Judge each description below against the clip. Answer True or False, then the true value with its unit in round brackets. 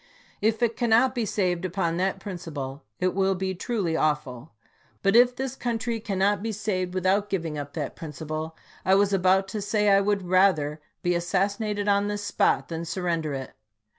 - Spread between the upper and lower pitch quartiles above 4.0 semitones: False (3.6 semitones)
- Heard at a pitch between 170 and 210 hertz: True (190 Hz)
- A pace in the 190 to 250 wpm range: False (180 wpm)